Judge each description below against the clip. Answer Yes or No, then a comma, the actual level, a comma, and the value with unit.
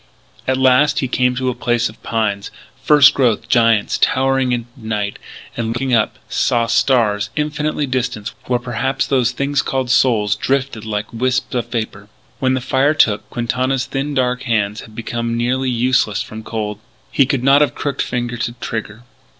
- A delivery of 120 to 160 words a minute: No, average, 170 wpm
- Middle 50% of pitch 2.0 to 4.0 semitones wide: Yes, average, 2.8 semitones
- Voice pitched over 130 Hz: No, low, 125 Hz